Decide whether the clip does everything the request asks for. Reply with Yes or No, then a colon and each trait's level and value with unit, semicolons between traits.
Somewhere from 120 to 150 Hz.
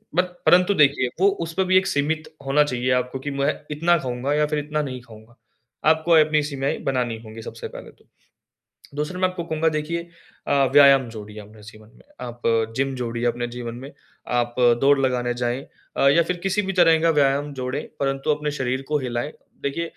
Yes: medium, 140 Hz